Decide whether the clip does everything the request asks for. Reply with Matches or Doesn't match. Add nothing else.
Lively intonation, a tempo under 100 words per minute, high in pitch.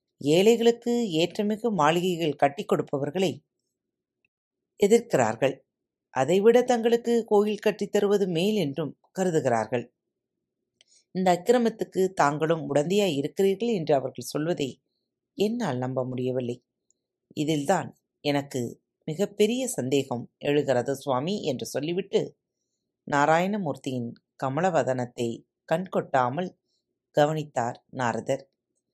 Doesn't match